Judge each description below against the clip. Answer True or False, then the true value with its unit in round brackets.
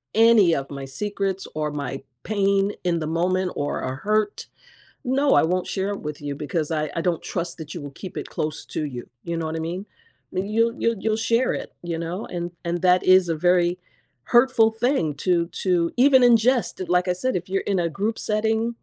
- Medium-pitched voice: True (180 Hz)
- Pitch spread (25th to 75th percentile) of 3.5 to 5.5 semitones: True (4.8 semitones)